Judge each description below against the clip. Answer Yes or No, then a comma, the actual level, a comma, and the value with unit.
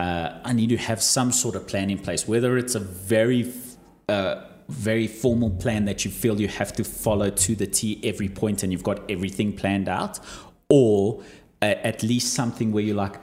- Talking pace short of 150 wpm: No, fast, 205 wpm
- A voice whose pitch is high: No, low, 110 Hz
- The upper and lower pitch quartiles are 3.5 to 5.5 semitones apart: No, average, 2.9 semitones